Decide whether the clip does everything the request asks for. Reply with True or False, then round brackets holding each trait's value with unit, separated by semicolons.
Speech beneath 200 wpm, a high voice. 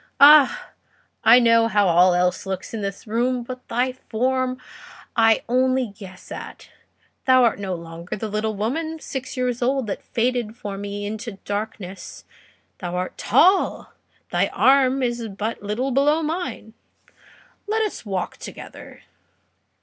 True (145 wpm; 230 Hz)